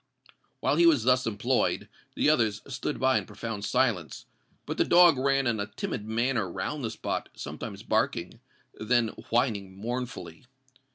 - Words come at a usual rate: Yes, average, 150 wpm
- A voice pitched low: Yes, low, 120 Hz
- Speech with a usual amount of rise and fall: Yes, average, 3.5 semitones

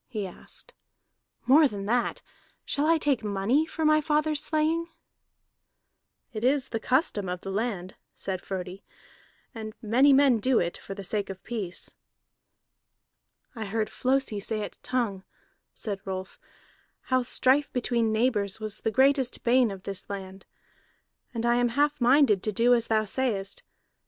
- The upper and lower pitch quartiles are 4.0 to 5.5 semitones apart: Yes, average, 4.9 semitones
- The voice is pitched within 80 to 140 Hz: No, high, 230 Hz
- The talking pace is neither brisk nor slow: Yes, average, 150 wpm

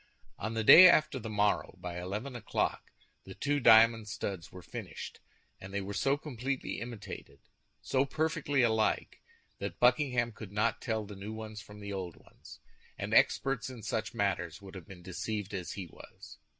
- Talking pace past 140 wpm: Yes, average, 175 wpm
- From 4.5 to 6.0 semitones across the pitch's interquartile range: No, average, 4.0 semitones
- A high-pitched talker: No, low, 110 Hz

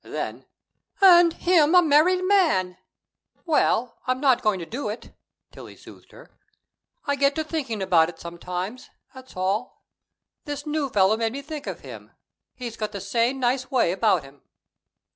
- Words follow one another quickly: No, average, 160 wpm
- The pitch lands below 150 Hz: No, very high, 255 Hz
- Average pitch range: No, wide, 7.2 semitones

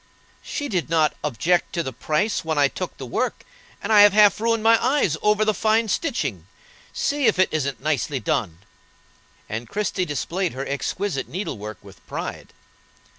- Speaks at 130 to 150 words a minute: No, average, 170 wpm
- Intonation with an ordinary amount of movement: No, wide, 7.2 semitones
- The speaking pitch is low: No, medium, 175 Hz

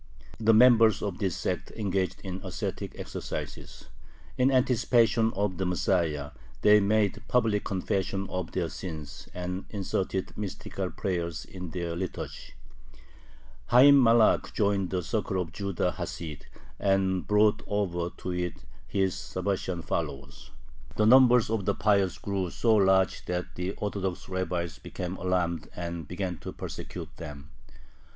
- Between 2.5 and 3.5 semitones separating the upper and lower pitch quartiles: Yes, average, 2.9 semitones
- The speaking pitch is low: Yes, very low, 95 Hz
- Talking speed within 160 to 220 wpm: No, slow, 135 wpm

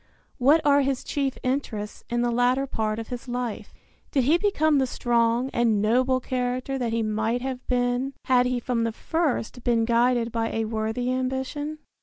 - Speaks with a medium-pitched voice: No, high, 245 Hz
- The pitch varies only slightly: Yes, narrow, 2.3 semitones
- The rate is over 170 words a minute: Yes, average, 180 wpm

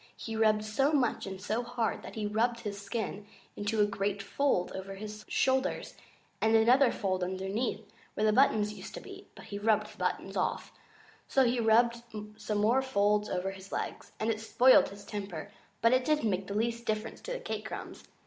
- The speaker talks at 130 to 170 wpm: No, average, 195 wpm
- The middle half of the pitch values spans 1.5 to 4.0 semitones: Yes, average, 2.7 semitones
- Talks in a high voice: Yes, high, 215 Hz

